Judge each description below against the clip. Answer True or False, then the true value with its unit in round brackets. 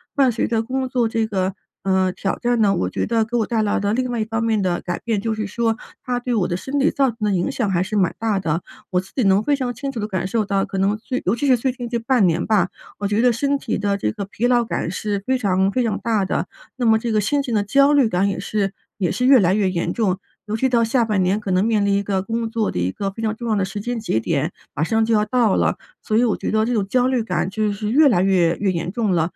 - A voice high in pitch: True (215 Hz)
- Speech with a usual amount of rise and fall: True (3.5 semitones)